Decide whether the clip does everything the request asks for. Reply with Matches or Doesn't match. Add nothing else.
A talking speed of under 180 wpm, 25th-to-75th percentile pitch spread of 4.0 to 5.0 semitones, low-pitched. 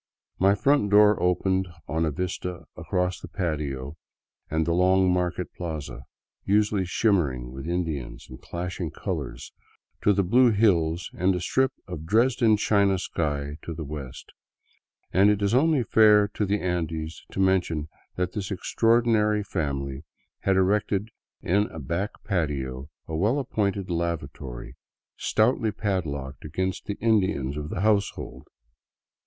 Matches